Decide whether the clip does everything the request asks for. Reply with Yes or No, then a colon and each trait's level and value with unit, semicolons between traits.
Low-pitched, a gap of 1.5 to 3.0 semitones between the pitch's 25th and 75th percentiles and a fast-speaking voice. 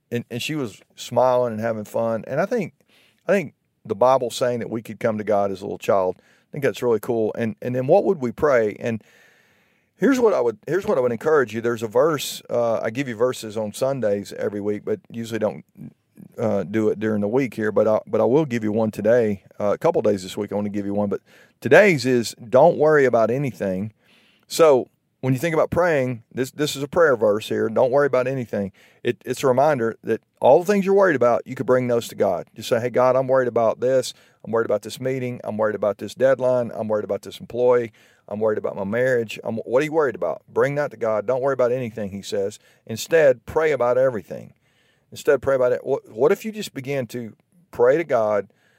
No: low, 120 Hz; average, 3.7 semitones; fast, 240 wpm